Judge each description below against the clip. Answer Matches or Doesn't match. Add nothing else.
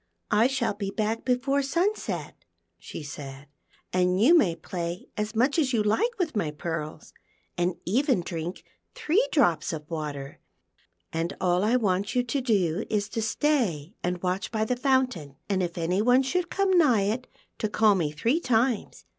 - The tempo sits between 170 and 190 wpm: Matches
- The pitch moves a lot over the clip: Matches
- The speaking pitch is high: Matches